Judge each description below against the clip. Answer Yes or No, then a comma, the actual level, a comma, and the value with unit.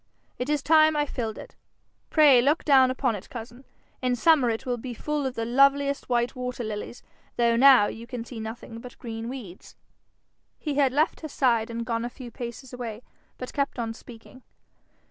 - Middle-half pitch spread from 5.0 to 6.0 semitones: No, average, 3.0 semitones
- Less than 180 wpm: No, average, 190 wpm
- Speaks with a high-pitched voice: Yes, very high, 250 Hz